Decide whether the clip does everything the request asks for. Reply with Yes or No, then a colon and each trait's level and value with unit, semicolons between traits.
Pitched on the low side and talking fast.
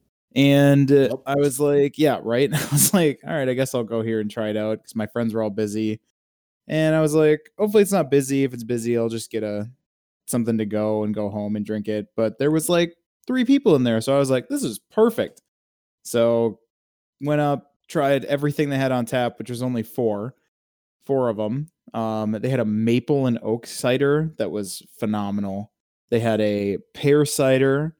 Yes: low, 120 Hz; fast, 210 wpm